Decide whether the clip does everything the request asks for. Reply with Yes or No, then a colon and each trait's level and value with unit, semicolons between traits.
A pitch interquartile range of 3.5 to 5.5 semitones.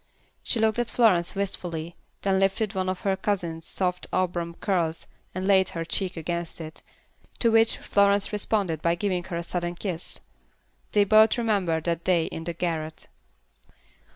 No: average, 3.1 semitones